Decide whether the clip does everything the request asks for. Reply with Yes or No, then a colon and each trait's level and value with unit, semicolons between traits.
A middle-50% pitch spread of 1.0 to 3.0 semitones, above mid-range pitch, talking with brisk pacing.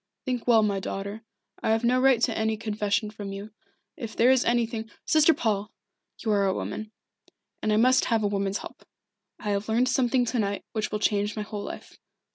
Yes: narrow, 2.5 semitones; high, 220 Hz; fast, 210 wpm